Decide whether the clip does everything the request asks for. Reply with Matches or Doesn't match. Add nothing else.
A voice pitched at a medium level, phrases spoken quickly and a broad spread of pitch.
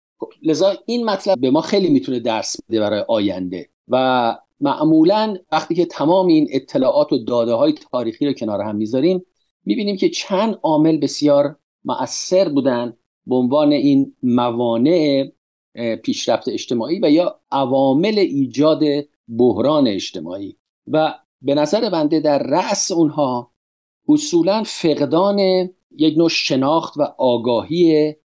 Doesn't match